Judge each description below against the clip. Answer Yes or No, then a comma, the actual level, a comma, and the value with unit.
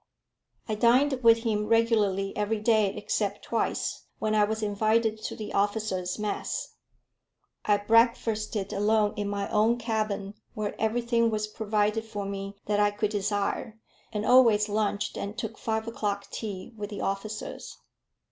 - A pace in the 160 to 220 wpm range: No, average, 145 wpm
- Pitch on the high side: Yes, high, 215 Hz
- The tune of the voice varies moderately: No, narrow, 1.5 semitones